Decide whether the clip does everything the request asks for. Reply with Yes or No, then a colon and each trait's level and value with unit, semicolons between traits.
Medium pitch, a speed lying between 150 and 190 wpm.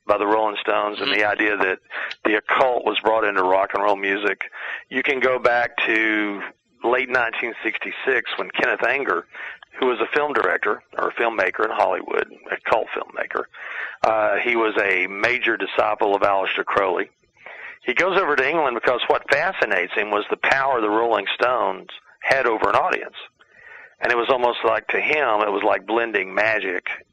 No: low, 115 Hz; average, 180 wpm